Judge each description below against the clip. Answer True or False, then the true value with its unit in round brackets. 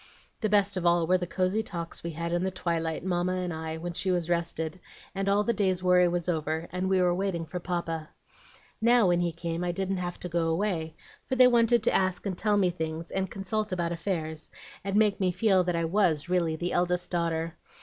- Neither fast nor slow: False (225 wpm)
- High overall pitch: False (180 Hz)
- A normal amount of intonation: False (2.3 semitones)